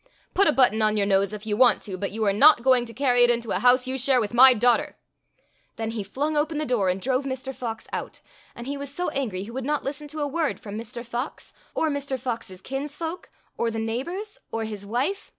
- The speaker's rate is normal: No, fast, 240 wpm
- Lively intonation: No, average, 4.1 semitones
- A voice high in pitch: Yes, very high, 250 Hz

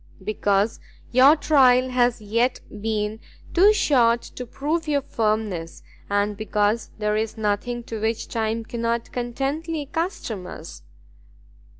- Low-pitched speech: No, high, 230 Hz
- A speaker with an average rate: No, slow, 120 wpm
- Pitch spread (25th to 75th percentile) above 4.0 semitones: No, average, 3.4 semitones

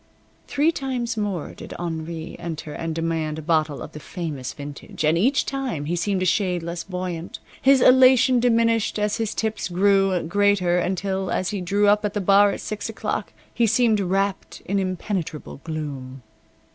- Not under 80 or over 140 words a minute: No, average, 170 wpm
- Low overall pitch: No, high, 190 Hz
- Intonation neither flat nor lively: Yes, average, 4.4 semitones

